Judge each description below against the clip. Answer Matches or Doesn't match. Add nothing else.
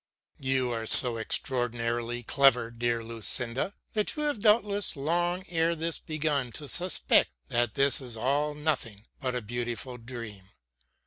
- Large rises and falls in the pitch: Doesn't match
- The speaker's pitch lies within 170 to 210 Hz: Doesn't match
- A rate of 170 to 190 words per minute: Doesn't match